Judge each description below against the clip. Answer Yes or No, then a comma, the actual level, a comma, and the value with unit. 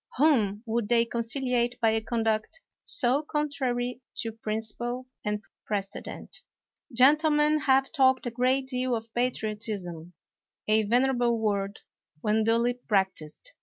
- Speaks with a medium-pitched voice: No, high, 235 Hz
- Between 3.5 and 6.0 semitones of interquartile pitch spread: No, average, 3.1 semitones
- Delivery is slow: Yes, slow, 125 wpm